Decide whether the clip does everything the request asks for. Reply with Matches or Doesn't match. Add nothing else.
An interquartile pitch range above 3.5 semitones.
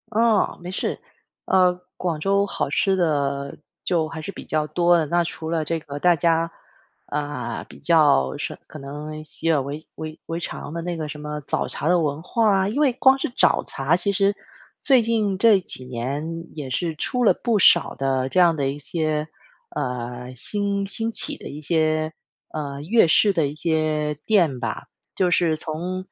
Matches